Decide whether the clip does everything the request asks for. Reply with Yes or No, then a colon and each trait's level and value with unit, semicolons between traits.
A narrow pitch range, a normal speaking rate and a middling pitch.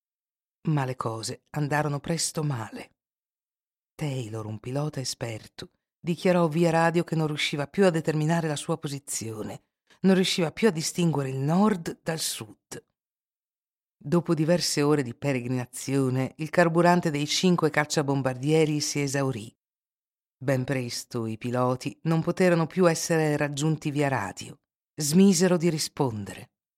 No: average, 4.2 semitones; average, 130 wpm; medium, 150 Hz